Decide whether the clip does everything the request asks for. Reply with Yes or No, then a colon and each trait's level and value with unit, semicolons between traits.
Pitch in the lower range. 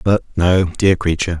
Yes: very low, 90 Hz